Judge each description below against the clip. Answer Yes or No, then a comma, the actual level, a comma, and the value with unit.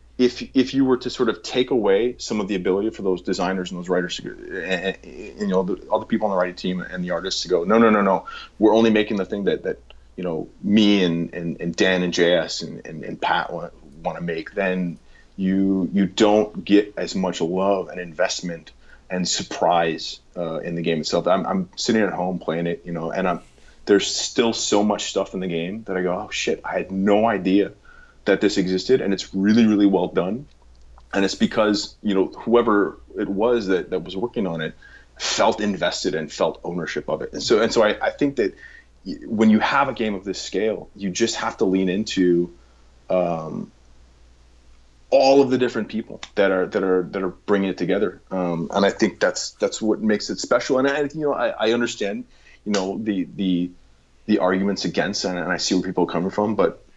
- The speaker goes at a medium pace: No, fast, 220 wpm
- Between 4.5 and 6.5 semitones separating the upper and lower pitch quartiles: No, average, 3.4 semitones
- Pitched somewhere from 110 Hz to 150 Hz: No, very low, 95 Hz